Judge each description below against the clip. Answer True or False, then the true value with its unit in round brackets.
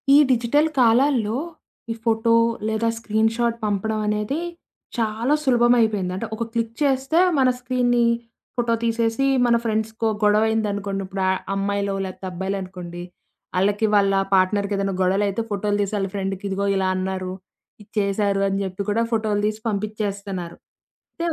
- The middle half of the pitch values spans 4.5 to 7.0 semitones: False (2.7 semitones)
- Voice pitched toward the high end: True (210 Hz)